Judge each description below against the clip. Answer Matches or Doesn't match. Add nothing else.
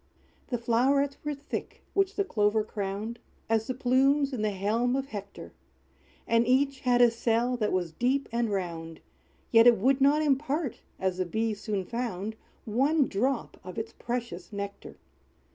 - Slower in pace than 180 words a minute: Matches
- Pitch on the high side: Matches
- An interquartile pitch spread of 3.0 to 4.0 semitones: Doesn't match